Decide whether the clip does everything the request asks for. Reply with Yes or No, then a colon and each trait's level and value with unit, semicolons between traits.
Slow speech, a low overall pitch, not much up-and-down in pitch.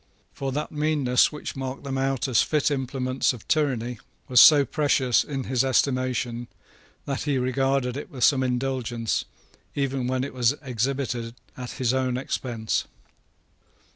No: average, 145 wpm; low, 130 Hz; narrow, 1.8 semitones